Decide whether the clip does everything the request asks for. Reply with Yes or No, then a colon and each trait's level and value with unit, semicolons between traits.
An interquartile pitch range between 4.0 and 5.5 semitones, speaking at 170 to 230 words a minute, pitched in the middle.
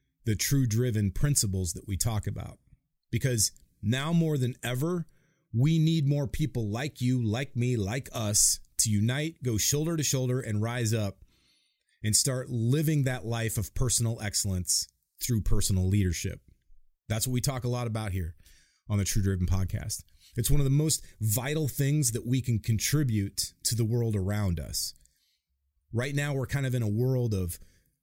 No: average, 5.2 semitones; average, 175 wpm; low, 115 Hz